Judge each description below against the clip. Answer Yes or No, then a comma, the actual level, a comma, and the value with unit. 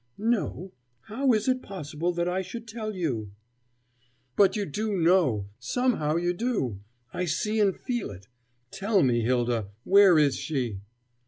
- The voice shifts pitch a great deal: Yes, wide, 8.3 semitones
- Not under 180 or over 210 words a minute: No, average, 155 wpm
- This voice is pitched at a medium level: Yes, medium, 180 Hz